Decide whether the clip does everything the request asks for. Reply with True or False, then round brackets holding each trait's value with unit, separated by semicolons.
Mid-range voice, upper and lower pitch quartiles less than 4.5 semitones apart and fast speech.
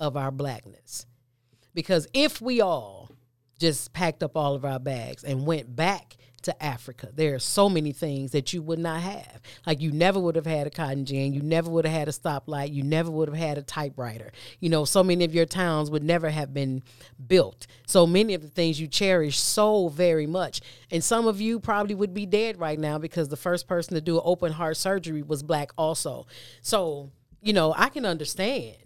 True (155 Hz; 4.1 semitones; 215 wpm)